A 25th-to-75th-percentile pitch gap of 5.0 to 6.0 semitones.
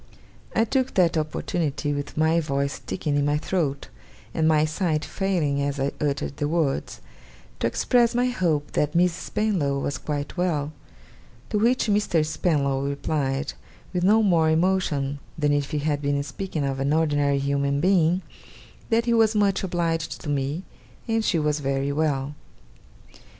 No: average, 4.2 semitones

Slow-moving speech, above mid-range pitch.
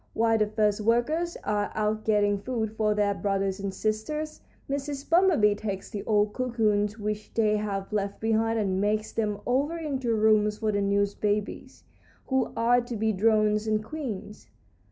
No: average, 165 wpm; high, 215 Hz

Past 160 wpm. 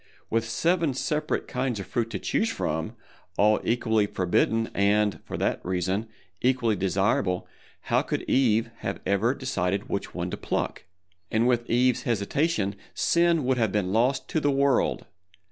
No: average, 155 wpm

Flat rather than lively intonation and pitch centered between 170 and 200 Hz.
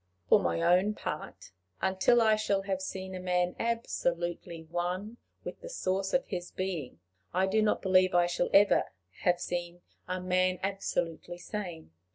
Yes: narrow, 2.0 semitones; medium, 185 Hz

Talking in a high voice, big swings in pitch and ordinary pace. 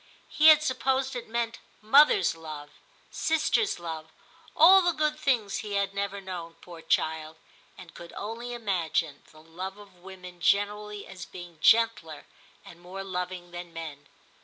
Yes: high, 195 Hz; wide, 5.8 semitones; average, 150 wpm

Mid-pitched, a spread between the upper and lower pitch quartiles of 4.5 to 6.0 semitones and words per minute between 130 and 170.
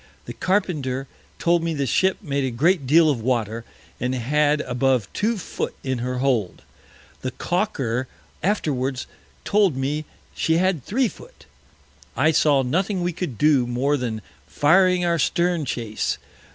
Yes: medium, 145 Hz; wide, 5.6 semitones; average, 150 wpm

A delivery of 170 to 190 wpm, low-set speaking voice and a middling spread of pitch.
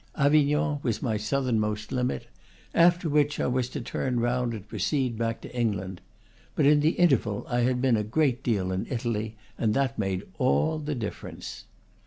Yes: average, 175 wpm; low, 125 Hz; average, 4.8 semitones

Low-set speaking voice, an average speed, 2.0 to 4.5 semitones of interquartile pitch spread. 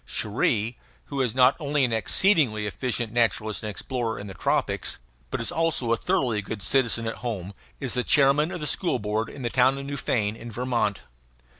Yes: low, 120 Hz; average, 190 wpm; average, 4.0 semitones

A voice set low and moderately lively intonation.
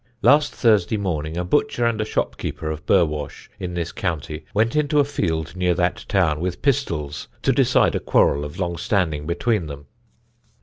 No: very low, 90 Hz; wide, 5.7 semitones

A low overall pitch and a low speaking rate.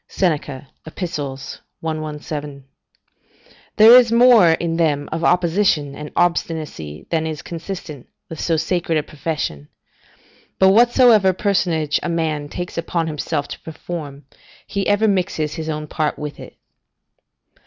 No: medium, 160 Hz; slow, 130 wpm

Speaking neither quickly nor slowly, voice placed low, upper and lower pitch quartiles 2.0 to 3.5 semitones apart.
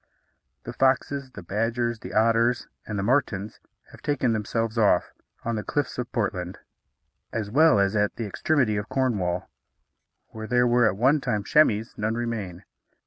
Yes: average, 160 wpm; low, 115 Hz; average, 2.9 semitones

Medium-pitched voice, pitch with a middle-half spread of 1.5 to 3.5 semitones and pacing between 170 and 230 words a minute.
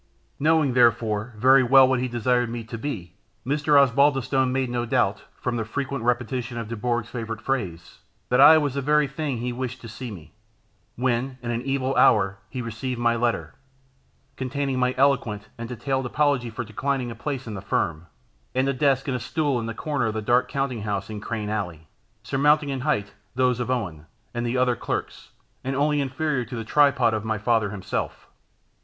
No: low, 125 Hz; average, 3.1 semitones; average, 190 wpm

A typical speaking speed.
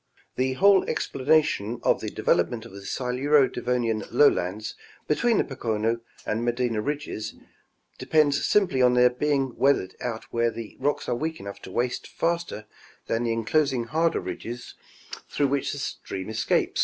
Yes: average, 155 wpm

